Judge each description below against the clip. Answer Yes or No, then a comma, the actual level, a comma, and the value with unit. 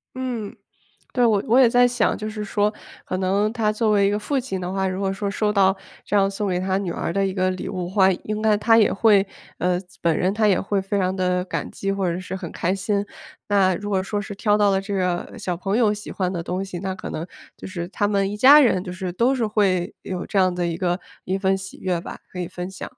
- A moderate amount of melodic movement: No, narrow, 2.2 semitones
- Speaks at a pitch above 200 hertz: No, high, 195 Hz